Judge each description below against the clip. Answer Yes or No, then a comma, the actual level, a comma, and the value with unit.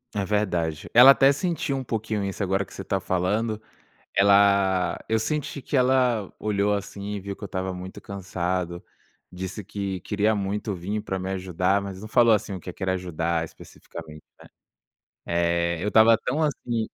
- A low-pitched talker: Yes, low, 100 Hz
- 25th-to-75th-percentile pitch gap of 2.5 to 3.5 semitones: Yes, average, 2.9 semitones